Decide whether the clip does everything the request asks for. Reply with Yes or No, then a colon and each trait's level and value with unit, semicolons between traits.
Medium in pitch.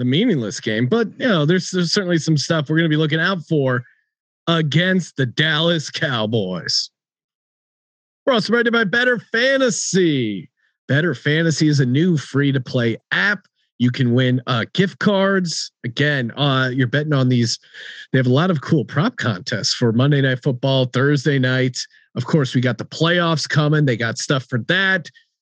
Yes: medium, 150 Hz